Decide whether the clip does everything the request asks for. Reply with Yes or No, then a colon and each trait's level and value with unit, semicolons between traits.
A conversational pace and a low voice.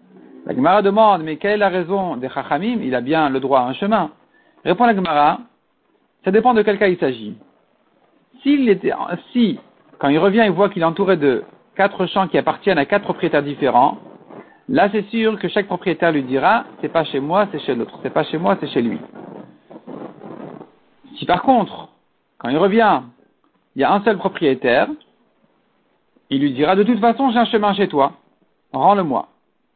No: average, 185 wpm; high, 195 Hz